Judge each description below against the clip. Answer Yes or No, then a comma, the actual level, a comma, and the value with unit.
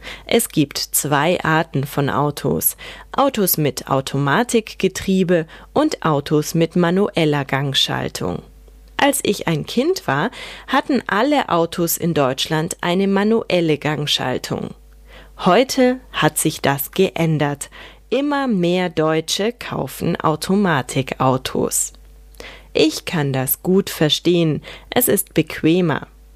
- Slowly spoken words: Yes, slow, 100 wpm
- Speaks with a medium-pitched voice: Yes, medium, 165 Hz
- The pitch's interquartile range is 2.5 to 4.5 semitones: No, average, 4.9 semitones